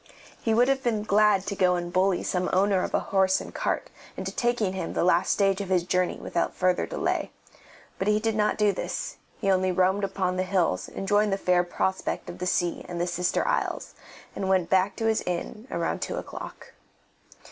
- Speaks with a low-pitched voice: No, high, 190 Hz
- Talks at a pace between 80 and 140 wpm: No, fast, 205 wpm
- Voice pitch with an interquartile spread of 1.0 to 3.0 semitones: Yes, narrow, 2.4 semitones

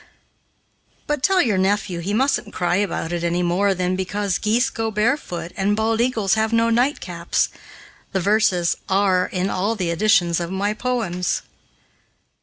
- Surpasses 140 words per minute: Yes, average, 155 wpm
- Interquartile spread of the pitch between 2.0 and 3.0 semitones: No, average, 3.7 semitones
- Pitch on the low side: No, high, 200 Hz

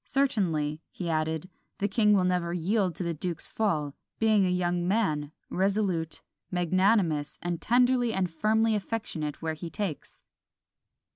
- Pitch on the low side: No, medium, 180 Hz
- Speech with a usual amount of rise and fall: Yes, average, 4.5 semitones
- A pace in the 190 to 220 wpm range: No, average, 140 wpm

